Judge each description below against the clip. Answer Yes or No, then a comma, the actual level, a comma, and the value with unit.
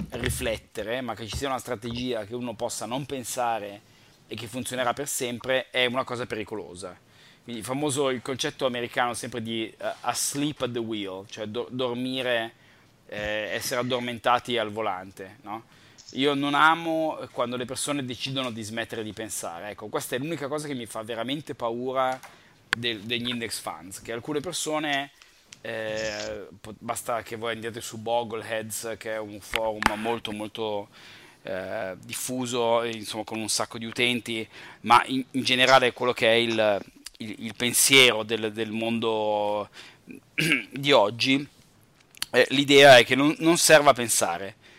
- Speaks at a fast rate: No, average, 155 wpm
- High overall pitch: No, low, 120 Hz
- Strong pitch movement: No, average, 2.9 semitones